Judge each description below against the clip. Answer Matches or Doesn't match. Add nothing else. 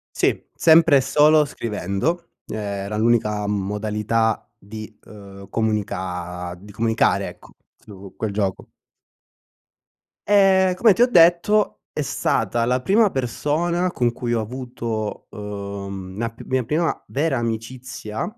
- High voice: Doesn't match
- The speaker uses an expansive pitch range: Matches